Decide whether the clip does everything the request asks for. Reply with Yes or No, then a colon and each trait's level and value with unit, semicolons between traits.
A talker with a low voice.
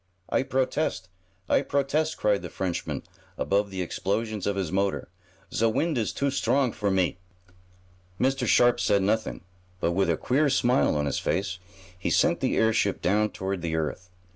Yes: low, 105 Hz